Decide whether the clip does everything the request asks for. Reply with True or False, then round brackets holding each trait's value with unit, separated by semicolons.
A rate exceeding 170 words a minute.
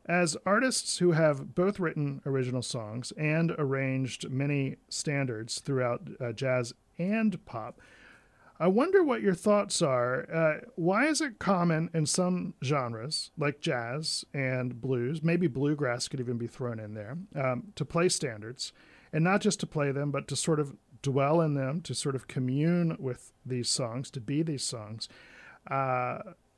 False (160 wpm)